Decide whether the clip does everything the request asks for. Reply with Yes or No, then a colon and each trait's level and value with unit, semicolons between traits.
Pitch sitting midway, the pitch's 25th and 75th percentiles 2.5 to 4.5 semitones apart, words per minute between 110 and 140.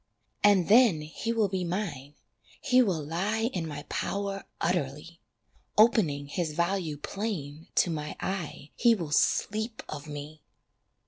No: medium, 175 Hz; wide, 5.5 semitones; slow, 135 wpm